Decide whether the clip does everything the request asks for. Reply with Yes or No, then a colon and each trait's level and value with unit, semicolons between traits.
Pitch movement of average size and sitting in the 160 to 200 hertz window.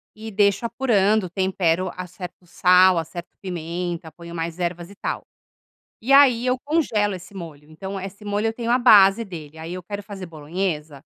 Yes: average, 3.5 semitones; medium, 185 Hz